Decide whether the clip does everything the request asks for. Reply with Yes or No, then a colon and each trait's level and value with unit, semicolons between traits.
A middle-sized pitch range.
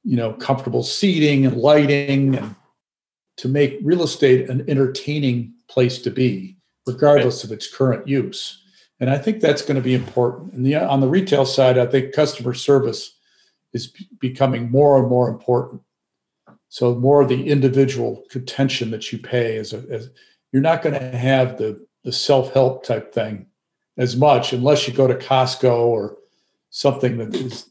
No: narrow, 2.2 semitones